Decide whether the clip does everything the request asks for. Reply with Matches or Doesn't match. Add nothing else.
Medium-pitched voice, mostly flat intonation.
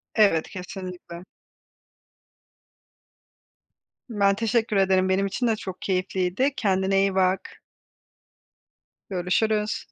Doesn't match